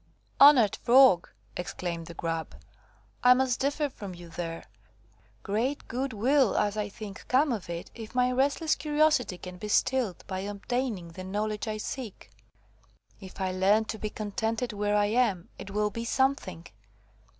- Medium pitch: No, high, 215 Hz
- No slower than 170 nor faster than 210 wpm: No, average, 160 wpm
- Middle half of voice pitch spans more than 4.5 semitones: Yes, average, 5.1 semitones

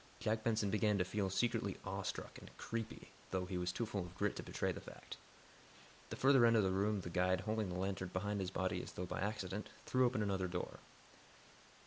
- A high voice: No, low, 100 Hz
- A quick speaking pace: Yes, fast, 220 wpm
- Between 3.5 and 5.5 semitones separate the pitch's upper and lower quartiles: No, average, 2.8 semitones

